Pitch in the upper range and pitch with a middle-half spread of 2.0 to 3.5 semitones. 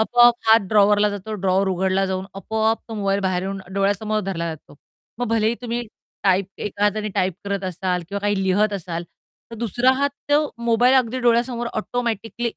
Yes: high, 205 Hz; average, 3.2 semitones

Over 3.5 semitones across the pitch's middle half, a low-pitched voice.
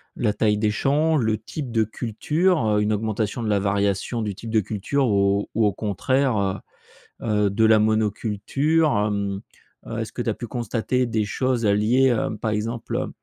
No: average, 2.7 semitones; low, 110 Hz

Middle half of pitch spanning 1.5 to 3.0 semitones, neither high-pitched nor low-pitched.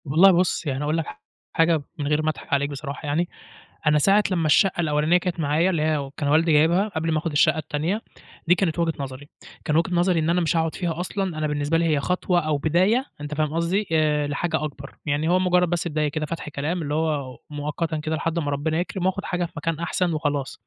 Yes: average, 2.7 semitones; medium, 160 Hz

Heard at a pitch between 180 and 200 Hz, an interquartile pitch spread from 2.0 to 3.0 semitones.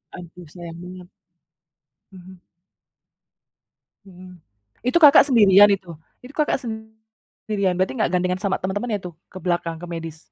No: medium, 185 Hz; average, 3.5 semitones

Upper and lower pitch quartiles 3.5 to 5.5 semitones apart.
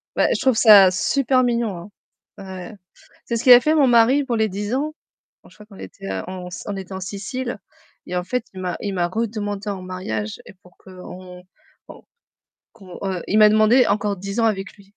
Yes: average, 3.8 semitones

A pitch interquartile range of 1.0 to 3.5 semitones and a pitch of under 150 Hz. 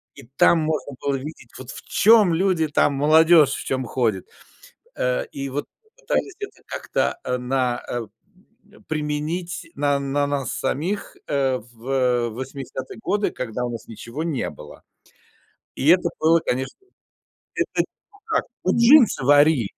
No: average, 4.3 semitones; medium, 140 Hz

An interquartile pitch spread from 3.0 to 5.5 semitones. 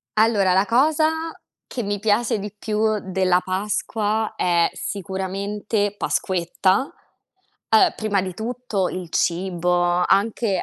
No: narrow, 2.6 semitones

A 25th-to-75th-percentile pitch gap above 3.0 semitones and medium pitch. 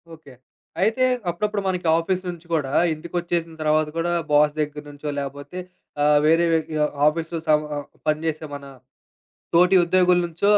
No: average, 2.7 semitones; medium, 165 Hz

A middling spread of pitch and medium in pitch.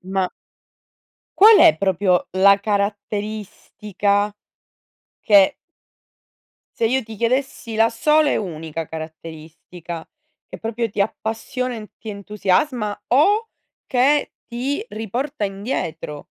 No: average, 4.2 semitones; high, 210 Hz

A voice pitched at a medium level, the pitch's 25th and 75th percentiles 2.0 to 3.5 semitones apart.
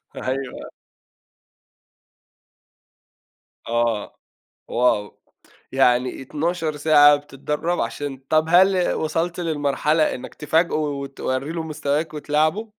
Yes: medium, 150 Hz; average, 3.1 semitones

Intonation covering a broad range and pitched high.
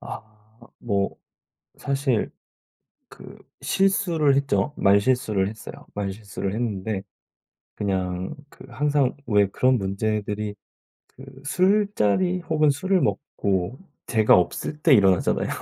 No: wide, 6.2 semitones; low, 110 Hz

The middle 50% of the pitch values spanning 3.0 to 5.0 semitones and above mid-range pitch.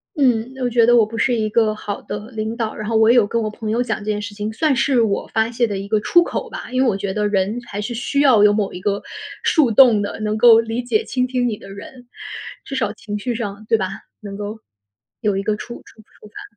No: narrow, 2.6 semitones; high, 220 Hz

